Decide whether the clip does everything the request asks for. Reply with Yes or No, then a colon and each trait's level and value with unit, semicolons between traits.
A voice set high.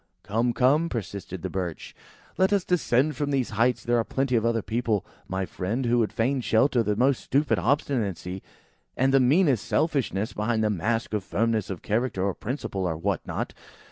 No: low, 115 Hz